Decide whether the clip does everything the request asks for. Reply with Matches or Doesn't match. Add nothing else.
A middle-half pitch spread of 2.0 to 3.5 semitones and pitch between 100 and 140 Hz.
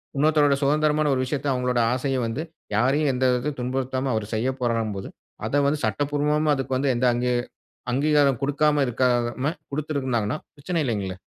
Matches